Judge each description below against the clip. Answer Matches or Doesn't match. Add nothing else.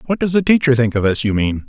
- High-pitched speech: Doesn't match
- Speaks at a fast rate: Matches